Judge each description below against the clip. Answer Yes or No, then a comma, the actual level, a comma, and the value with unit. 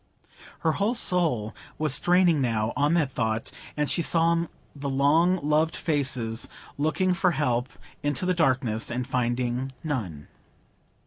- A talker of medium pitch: Yes, medium, 145 Hz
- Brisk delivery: No, slow, 135 wpm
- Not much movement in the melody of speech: No, average, 5.2 semitones